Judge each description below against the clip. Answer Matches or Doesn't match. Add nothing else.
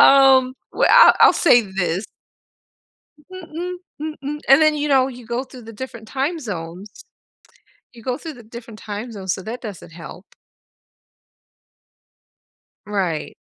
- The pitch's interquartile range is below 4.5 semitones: Doesn't match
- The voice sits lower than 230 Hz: Doesn't match